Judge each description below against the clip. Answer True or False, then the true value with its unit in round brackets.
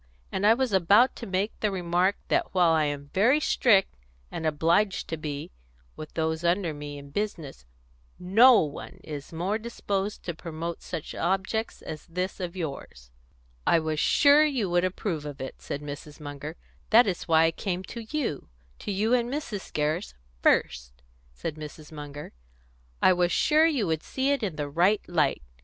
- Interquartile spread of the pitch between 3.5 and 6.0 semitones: True (5.3 semitones)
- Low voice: False (175 Hz)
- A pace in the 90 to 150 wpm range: False (175 wpm)